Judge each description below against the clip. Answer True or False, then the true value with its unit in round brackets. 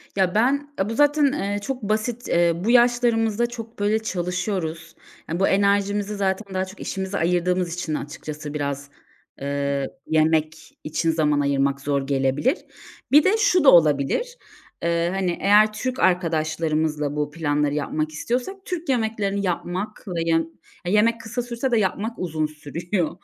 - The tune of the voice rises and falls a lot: True (6.0 semitones)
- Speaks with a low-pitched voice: False (185 Hz)